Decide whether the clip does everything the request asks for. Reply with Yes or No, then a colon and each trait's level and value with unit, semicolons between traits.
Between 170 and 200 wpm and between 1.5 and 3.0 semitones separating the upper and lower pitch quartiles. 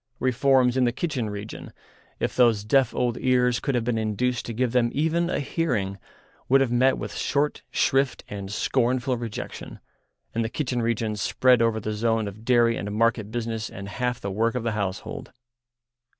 Yes: average, 180 wpm; average, 2.7 semitones